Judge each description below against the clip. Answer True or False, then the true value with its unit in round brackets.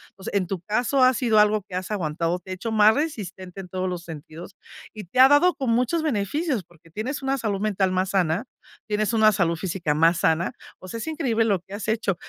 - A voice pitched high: True (200 Hz)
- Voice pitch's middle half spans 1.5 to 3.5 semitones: False (4.3 semitones)